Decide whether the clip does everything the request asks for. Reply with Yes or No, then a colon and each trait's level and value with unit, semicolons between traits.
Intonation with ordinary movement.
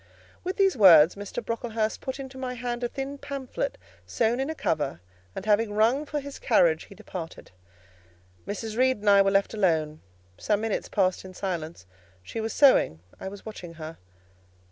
No: wide, 5.7 semitones